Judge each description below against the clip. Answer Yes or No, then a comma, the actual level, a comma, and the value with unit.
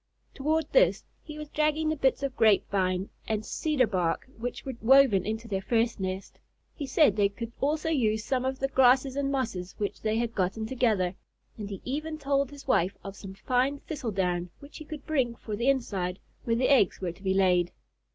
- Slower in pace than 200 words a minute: No, fast, 205 wpm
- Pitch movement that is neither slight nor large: No, wide, 5.9 semitones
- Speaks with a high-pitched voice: Yes, high, 235 Hz